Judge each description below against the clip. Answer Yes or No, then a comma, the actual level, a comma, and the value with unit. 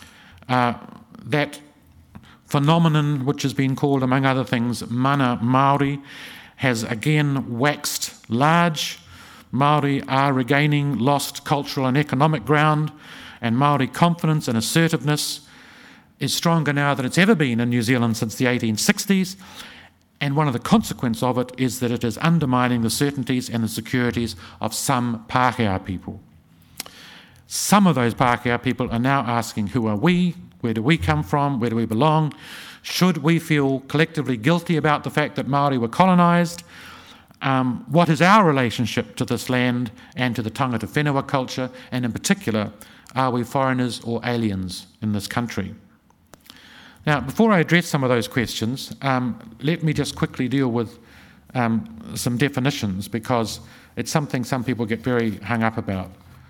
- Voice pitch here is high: No, low, 130 Hz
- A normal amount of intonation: Yes, average, 4.0 semitones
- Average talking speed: Yes, average, 155 wpm